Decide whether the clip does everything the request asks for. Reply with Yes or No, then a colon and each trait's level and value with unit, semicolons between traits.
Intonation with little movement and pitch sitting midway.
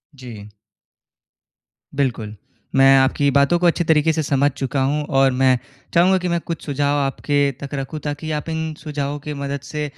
Yes: narrow, 2.2 semitones; medium, 145 Hz